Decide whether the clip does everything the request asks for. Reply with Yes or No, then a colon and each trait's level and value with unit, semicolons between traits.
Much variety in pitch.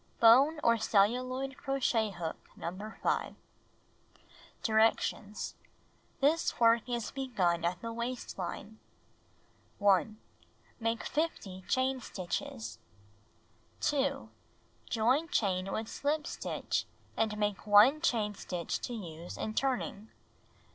No: average, 4.3 semitones